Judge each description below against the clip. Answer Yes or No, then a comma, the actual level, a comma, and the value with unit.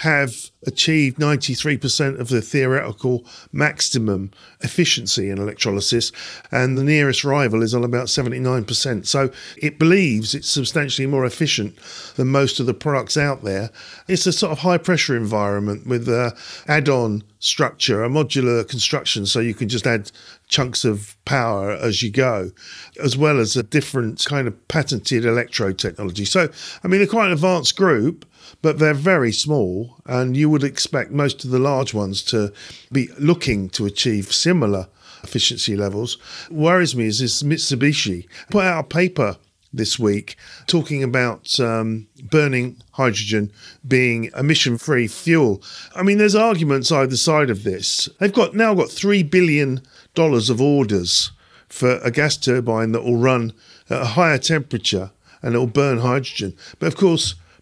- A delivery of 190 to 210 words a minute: No, average, 160 wpm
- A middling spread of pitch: Yes, average, 4.7 semitones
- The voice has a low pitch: Yes, low, 130 Hz